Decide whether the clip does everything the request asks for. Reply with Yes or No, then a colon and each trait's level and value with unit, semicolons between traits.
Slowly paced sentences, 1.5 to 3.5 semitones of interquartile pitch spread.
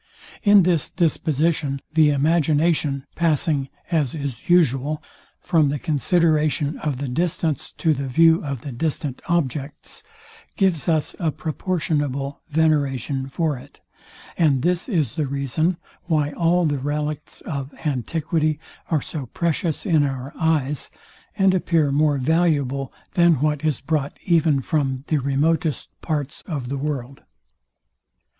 Yes: slow, 130 wpm; average, 2.9 semitones